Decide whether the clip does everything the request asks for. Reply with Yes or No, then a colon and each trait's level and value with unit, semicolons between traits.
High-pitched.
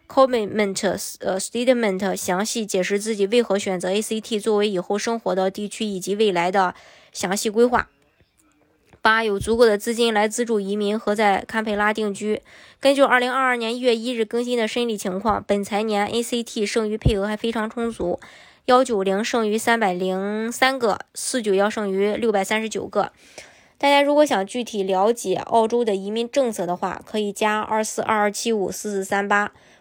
Yes: high, 215 Hz